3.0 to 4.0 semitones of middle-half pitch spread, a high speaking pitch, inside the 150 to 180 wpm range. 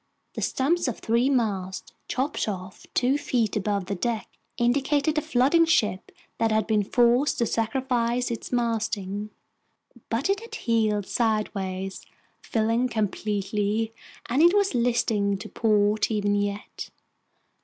No: average, 3.3 semitones; high, 225 Hz; slow, 135 wpm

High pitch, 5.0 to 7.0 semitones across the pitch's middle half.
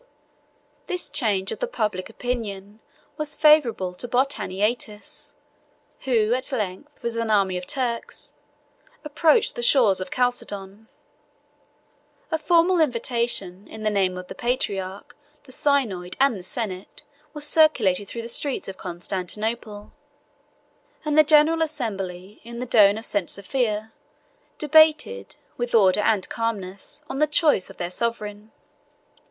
Yes: high, 225 Hz; wide, 5.4 semitones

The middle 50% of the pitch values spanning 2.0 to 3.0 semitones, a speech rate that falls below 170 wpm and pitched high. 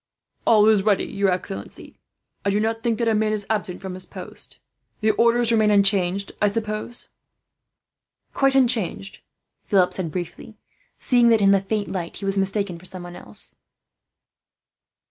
Yes: narrow, 2.6 semitones; average, 160 wpm; high, 205 Hz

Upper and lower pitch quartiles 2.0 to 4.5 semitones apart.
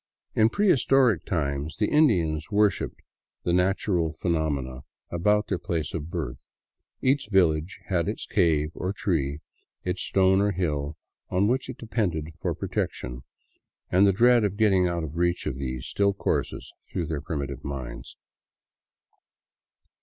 No: average, 4.9 semitones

